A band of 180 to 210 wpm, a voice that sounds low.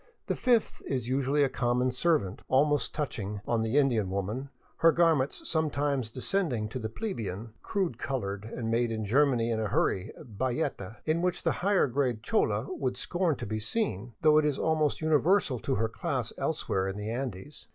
Yes: average, 185 wpm; low, 130 Hz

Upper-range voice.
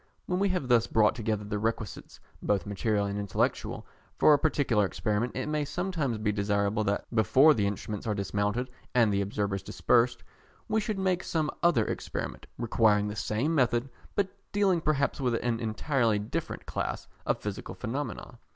No: low, 115 Hz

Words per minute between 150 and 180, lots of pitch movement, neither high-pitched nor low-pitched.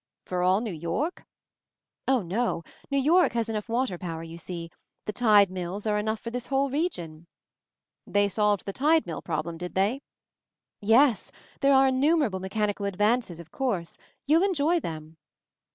No: average, 170 wpm; wide, 7.0 semitones; high, 210 Hz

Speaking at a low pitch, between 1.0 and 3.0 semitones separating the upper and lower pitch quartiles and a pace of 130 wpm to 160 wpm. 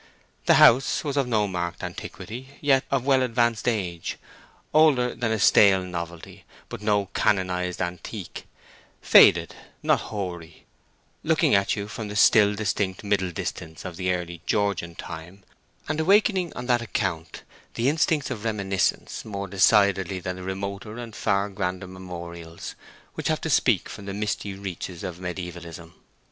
No: low, 100 Hz; average, 3.9 semitones; average, 150 wpm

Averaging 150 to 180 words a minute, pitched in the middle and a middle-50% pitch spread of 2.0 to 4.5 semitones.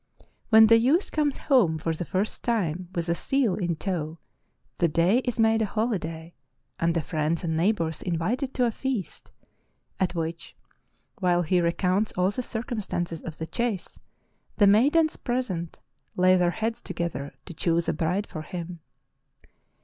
No: average, 165 wpm; medium, 180 Hz; average, 5.1 semitones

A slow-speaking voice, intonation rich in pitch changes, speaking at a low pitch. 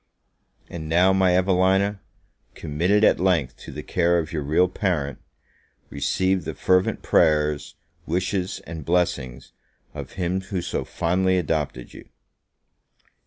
No: slow, 125 wpm; average, 3.3 semitones; very low, 90 Hz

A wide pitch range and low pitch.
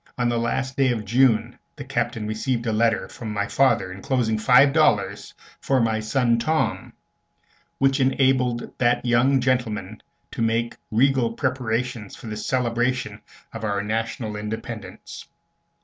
No: average, 2.9 semitones; low, 120 Hz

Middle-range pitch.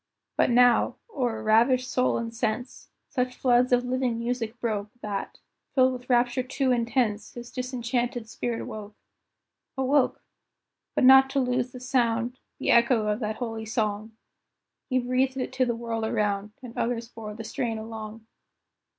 No: high, 240 Hz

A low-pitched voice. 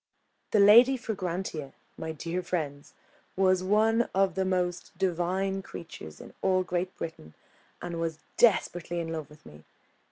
No: medium, 180 Hz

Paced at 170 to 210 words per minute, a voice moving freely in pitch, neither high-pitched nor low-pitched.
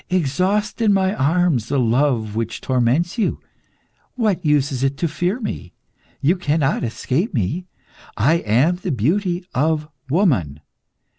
No: average, 140 wpm; wide, 6.1 semitones; medium, 150 Hz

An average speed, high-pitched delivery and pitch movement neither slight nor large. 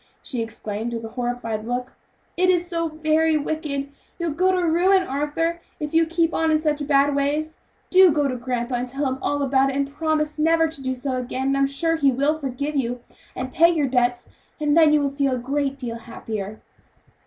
No: fast, 215 wpm; very high, 285 Hz; average, 3.8 semitones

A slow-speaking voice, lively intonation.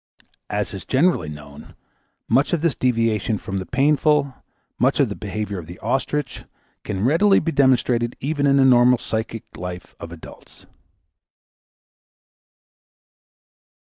Yes: slow, 130 wpm; wide, 6.0 semitones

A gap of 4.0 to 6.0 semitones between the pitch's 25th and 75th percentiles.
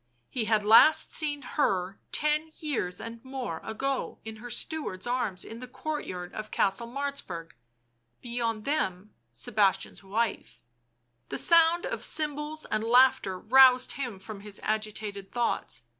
Yes: wide, 5.6 semitones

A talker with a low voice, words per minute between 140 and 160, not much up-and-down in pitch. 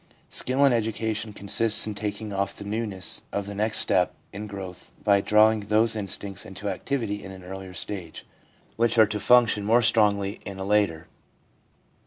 No: low, 105 Hz; average, 170 wpm; narrow, 2.0 semitones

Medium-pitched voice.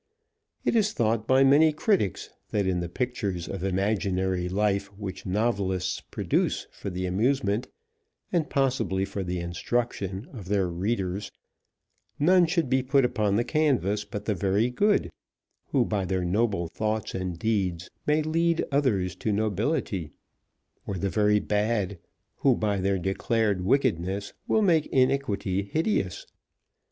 No: low, 105 Hz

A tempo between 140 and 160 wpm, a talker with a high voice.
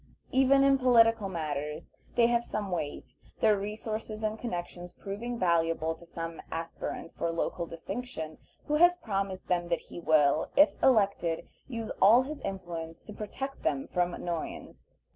Yes: average, 150 wpm; high, 195 Hz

